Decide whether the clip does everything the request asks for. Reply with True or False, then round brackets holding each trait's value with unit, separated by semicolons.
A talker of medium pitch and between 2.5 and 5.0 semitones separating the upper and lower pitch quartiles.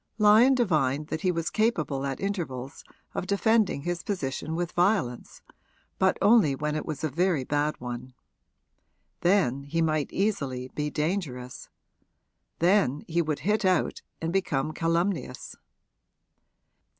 False (165 Hz; 5.6 semitones)